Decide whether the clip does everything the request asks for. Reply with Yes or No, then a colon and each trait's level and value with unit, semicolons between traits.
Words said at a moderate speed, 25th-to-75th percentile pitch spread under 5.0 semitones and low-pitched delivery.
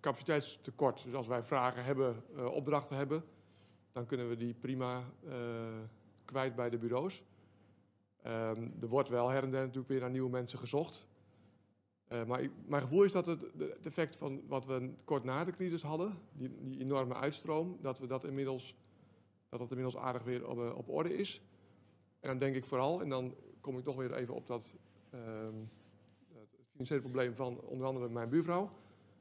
Yes: average, 185 wpm; average, 3.4 semitones; low, 130 Hz